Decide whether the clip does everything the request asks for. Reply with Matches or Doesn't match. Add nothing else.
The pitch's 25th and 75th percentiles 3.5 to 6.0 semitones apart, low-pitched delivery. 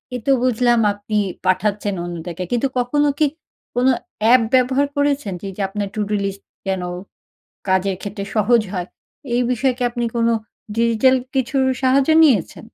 Doesn't match